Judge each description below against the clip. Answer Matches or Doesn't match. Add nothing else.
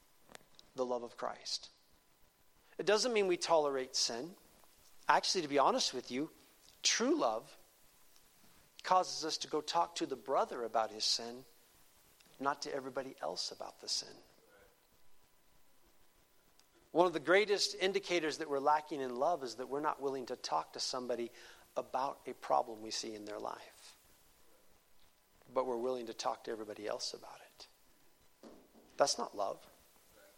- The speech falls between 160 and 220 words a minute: Doesn't match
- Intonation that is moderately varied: Doesn't match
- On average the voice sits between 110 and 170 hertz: Matches